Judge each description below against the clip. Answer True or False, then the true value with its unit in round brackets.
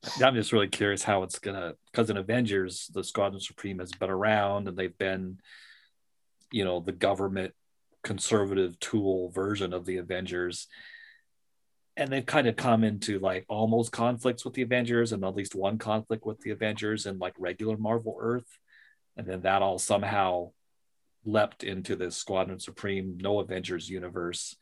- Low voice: True (100 Hz)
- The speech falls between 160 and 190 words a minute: True (165 wpm)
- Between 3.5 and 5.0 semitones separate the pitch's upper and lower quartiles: False (3.1 semitones)